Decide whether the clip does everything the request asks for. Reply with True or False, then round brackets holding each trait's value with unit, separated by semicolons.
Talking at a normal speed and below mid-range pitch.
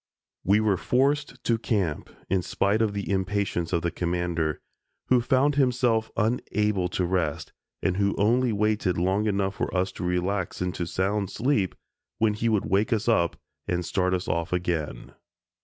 True (165 wpm; 100 Hz)